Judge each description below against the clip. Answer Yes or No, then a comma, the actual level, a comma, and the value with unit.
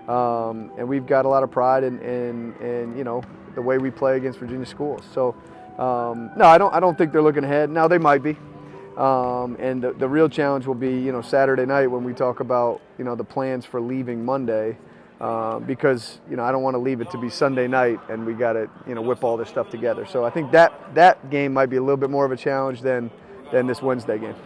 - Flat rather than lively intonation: Yes, narrow, 2.0 semitones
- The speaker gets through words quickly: Yes, fast, 255 wpm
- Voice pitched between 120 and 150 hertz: Yes, low, 130 Hz